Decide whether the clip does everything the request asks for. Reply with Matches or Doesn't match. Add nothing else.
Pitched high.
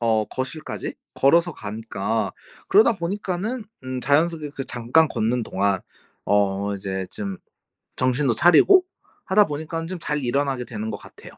Doesn't match